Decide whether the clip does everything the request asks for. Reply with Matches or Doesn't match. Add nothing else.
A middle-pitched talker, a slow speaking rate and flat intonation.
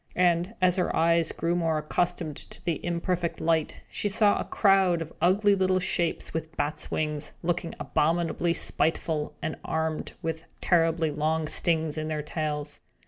Doesn't match